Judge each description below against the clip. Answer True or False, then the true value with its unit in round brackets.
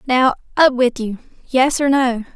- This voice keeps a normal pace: True (180 wpm)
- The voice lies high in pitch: True (255 Hz)